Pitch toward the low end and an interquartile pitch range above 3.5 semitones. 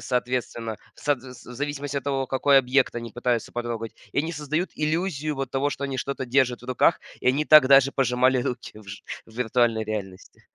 No: low, 130 Hz; average, 2.9 semitones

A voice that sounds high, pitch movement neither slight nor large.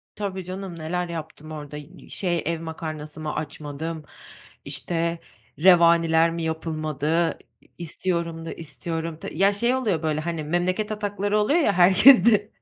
No: medium, 165 Hz; average, 3.1 semitones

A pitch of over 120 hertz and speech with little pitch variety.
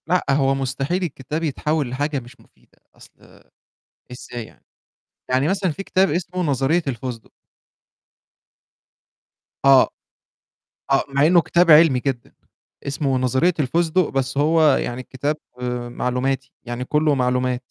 No: low, 135 Hz; average, 3.7 semitones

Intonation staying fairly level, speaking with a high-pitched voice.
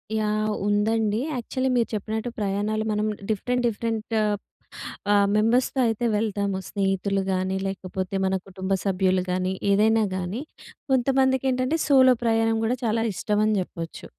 No: average, 3.0 semitones; high, 215 Hz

